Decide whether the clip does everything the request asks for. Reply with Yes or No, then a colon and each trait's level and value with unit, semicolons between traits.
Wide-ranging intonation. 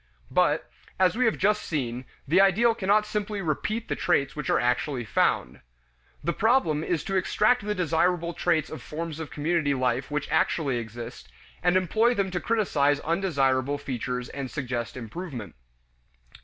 Yes: wide, 6.6 semitones